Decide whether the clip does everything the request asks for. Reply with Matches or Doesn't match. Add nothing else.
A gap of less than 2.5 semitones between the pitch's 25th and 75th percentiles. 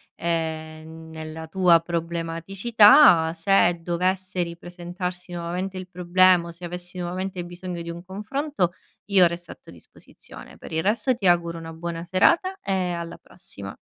Matches